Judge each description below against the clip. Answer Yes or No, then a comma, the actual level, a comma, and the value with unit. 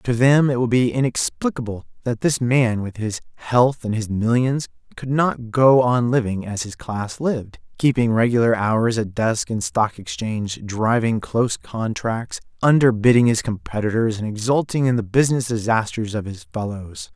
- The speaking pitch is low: Yes, low, 115 Hz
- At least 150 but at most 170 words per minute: Yes, average, 165 wpm